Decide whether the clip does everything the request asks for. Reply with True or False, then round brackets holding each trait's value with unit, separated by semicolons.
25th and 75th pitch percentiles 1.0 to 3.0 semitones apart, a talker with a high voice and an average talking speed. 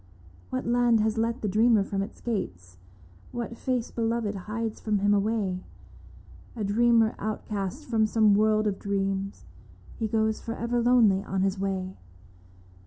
True (2.7 semitones; 215 Hz; 155 wpm)